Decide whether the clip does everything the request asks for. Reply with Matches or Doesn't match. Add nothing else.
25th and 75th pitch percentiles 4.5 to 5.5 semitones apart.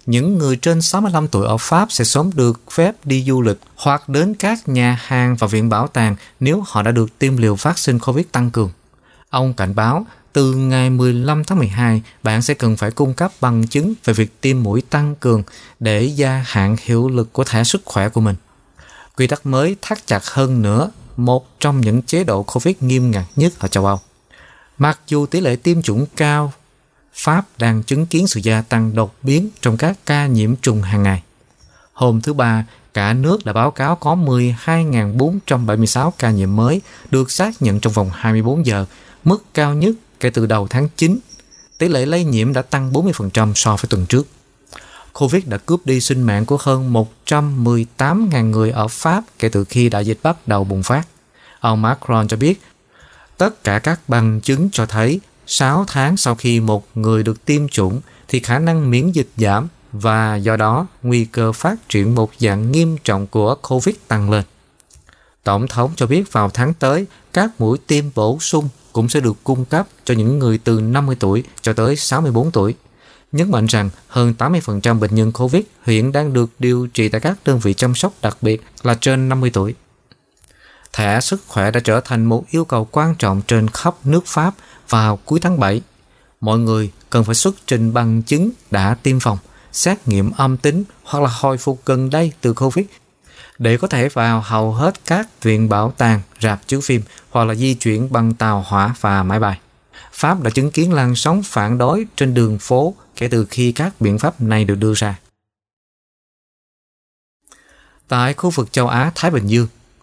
Matches